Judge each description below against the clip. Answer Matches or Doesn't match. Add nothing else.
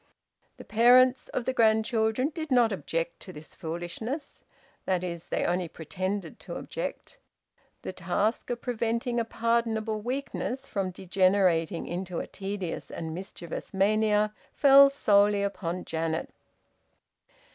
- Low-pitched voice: Doesn't match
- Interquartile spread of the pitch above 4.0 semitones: Matches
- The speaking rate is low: Matches